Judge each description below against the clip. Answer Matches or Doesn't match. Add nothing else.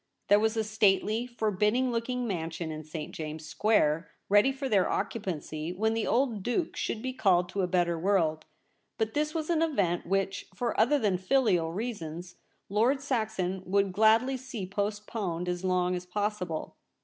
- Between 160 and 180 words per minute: Matches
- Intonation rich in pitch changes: Doesn't match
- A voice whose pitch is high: Matches